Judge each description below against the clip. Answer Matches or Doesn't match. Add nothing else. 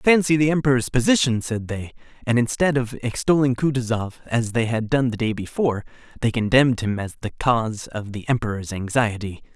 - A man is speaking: Matches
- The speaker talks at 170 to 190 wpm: Matches